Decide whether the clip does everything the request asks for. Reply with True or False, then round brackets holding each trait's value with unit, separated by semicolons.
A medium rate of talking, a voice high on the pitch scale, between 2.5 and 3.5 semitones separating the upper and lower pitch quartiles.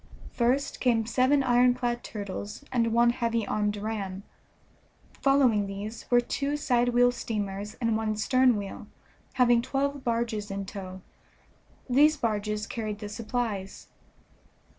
False (125 wpm; 230 Hz; 3.1 semitones)